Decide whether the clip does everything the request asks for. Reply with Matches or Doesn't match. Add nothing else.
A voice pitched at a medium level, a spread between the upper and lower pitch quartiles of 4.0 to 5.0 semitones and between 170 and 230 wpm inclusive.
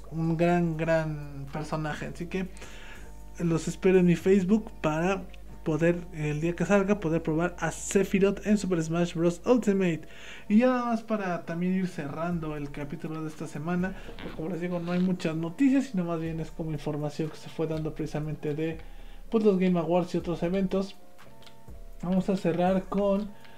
Doesn't match